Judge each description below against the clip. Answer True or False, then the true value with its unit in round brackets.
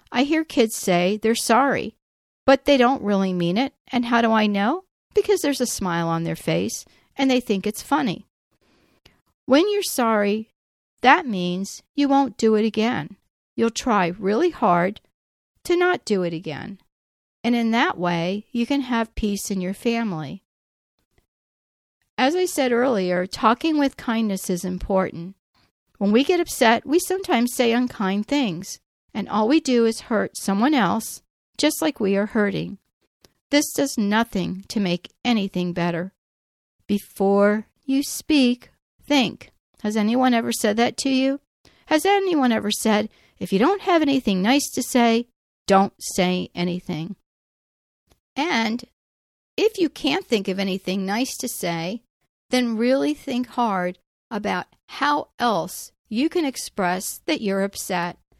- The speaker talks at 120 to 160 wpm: True (150 wpm)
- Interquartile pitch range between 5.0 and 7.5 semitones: True (5.5 semitones)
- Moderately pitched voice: False (225 Hz)